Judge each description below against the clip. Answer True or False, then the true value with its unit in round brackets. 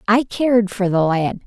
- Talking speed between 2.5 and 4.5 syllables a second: False (4.7 syllables/s)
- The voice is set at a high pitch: True (205 Hz)